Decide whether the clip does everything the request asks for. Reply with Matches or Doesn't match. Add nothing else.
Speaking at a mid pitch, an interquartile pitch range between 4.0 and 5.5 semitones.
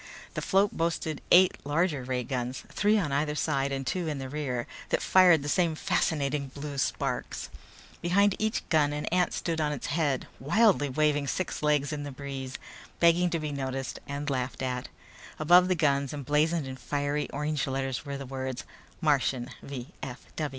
Doesn't match